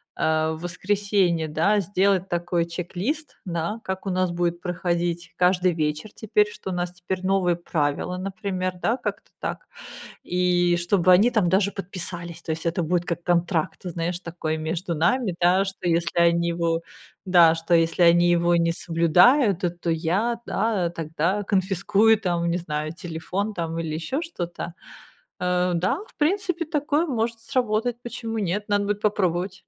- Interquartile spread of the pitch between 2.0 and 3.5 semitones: Yes, average, 3.0 semitones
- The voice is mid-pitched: Yes, medium, 180 Hz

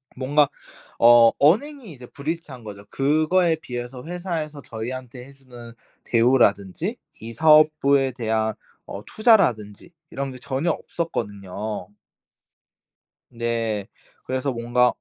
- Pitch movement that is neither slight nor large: Yes, average, 4.9 semitones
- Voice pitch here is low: Yes, low, 130 Hz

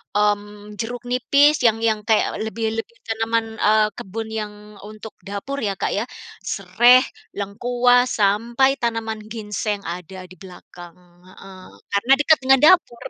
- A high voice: Yes, high, 220 Hz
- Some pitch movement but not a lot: Yes, average, 3.1 semitones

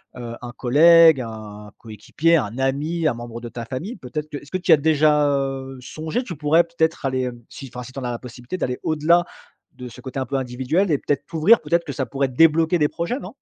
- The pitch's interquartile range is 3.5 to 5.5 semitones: Yes, average, 4.5 semitones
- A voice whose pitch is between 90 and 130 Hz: No, medium, 140 Hz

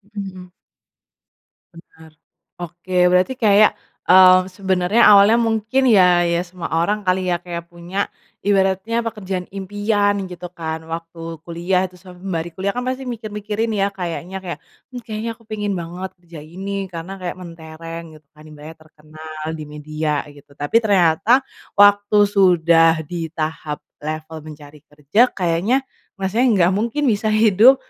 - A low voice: No, medium, 185 Hz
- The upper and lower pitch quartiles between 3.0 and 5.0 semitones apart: Yes, average, 3.7 semitones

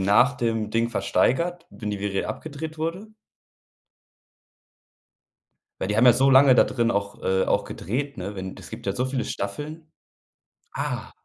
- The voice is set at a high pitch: No, low, 120 Hz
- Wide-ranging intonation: Yes, wide, 5.9 semitones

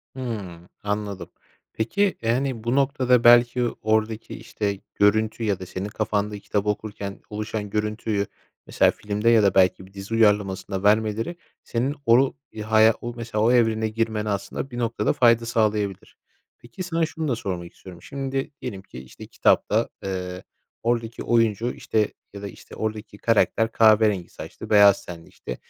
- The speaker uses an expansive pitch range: No, narrow, 2.5 semitones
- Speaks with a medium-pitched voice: No, low, 110 Hz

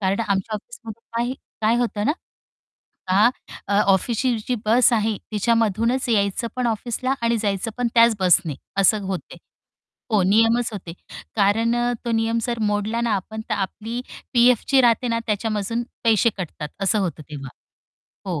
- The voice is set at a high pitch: Yes, high, 220 Hz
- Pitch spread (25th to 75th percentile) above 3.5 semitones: No, average, 2.8 semitones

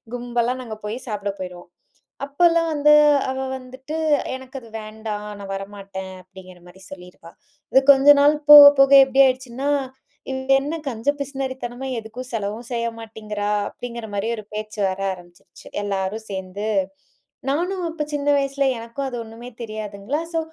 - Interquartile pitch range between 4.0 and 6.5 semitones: Yes, average, 4.9 semitones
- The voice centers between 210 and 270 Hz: Yes, high, 235 Hz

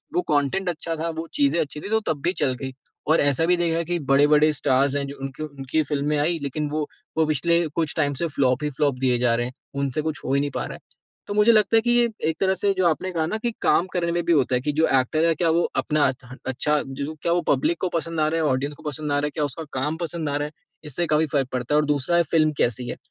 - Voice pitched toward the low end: No, medium, 150 Hz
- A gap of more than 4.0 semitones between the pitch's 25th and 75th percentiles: No, average, 3.1 semitones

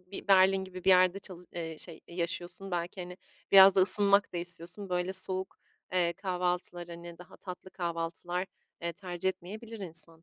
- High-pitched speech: No, medium, 180 Hz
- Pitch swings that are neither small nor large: No, narrow, 1.7 semitones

